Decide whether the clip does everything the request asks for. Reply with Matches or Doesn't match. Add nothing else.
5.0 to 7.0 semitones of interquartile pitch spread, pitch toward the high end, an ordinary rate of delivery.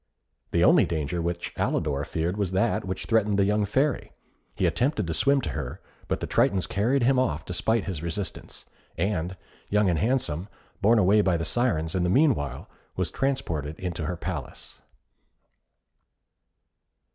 Doesn't match